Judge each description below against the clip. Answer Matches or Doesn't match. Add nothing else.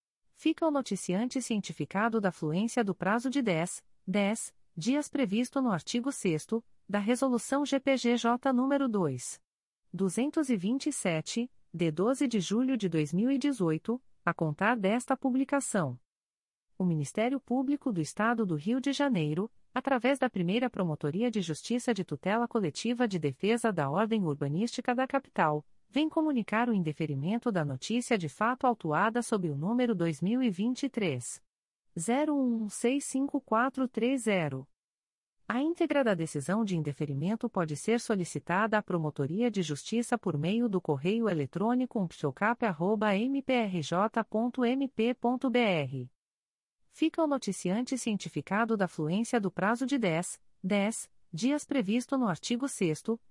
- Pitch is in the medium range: Doesn't match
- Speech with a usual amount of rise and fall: Doesn't match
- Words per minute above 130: Doesn't match